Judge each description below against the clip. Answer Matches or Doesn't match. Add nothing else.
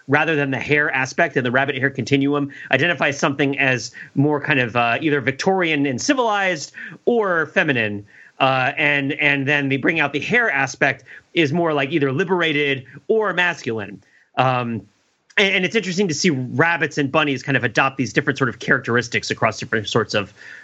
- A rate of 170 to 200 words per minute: Matches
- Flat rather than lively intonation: Doesn't match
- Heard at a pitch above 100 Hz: Matches